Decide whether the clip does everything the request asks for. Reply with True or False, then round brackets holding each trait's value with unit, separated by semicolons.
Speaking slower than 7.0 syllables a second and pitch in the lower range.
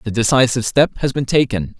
True (6.3 syllables/s; 120 Hz)